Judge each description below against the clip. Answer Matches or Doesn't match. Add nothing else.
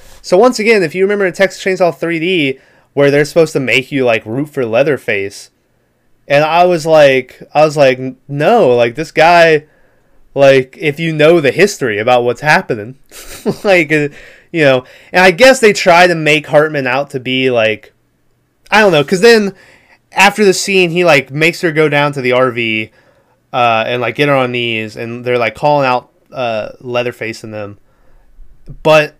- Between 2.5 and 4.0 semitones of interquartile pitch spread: Doesn't match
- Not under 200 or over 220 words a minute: Doesn't match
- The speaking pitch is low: Doesn't match